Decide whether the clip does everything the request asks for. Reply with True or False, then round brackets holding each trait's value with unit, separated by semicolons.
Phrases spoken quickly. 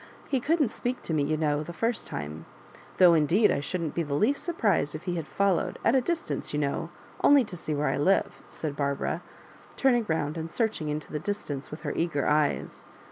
True (215 wpm)